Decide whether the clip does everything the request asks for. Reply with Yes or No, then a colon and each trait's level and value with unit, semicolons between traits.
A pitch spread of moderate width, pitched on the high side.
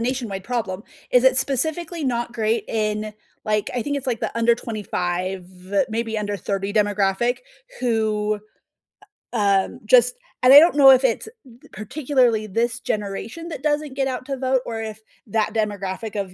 Yes: average, 3.9 semitones; high, 230 Hz